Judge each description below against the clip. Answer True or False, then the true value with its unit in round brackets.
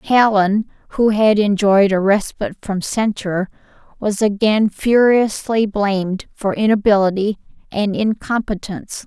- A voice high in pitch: True (205 Hz)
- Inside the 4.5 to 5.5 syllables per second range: False (4.3 syllables/s)